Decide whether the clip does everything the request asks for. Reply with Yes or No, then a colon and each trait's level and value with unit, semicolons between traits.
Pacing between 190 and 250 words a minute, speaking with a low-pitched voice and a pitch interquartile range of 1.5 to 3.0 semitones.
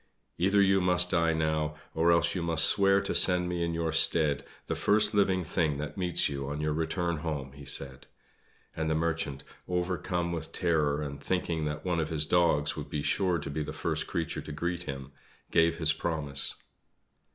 Yes: average, 195 wpm; very low, 80 Hz; average, 2.7 semitones